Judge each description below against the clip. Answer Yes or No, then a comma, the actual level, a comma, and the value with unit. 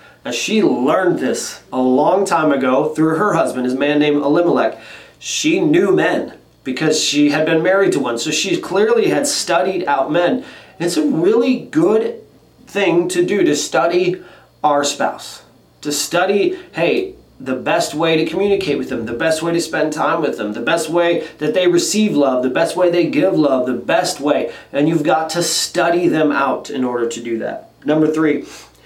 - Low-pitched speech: No, medium, 160 Hz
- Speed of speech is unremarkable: Yes, average, 190 wpm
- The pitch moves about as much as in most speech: No, wide, 6.5 semitones